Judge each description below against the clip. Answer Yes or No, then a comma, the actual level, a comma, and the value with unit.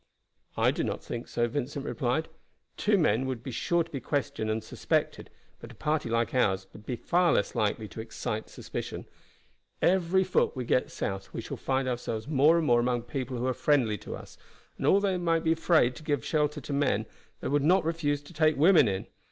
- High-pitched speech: No, low, 135 Hz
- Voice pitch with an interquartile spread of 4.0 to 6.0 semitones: Yes, average, 5.2 semitones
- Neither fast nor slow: No, fast, 210 wpm